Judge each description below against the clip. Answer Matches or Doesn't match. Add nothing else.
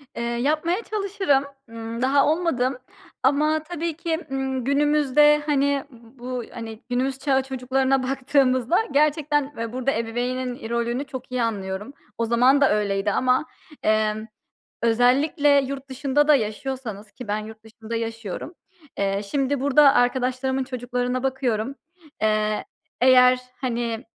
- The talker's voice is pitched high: Matches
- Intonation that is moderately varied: Matches